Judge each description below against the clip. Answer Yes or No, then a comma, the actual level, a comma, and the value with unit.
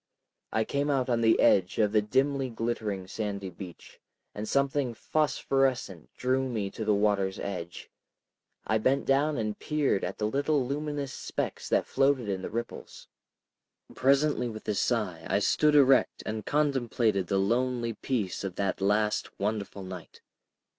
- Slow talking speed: No, average, 155 wpm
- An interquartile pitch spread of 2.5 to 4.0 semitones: No, average, 5.2 semitones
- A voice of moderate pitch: No, low, 115 Hz